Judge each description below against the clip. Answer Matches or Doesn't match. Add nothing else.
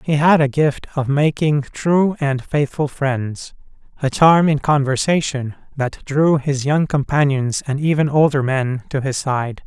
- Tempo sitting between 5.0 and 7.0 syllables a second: Doesn't match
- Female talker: Doesn't match